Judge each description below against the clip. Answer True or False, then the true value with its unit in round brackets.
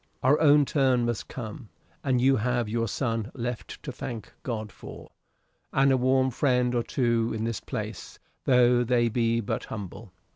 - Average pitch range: False (2.2 semitones)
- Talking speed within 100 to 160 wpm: False (170 wpm)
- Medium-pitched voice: False (120 Hz)